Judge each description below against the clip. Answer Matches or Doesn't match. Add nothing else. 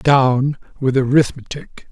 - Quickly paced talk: Doesn't match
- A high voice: Doesn't match